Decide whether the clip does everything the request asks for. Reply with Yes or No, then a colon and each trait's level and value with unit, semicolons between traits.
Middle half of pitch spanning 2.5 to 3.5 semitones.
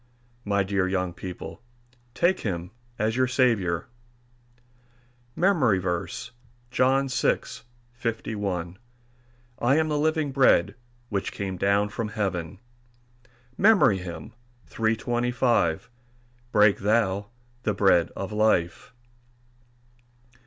No: average, 4.4 semitones